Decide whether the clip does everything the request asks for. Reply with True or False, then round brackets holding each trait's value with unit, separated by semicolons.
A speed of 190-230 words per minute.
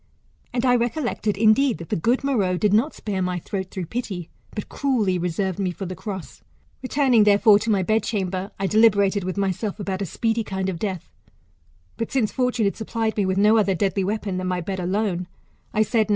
True (200 wpm)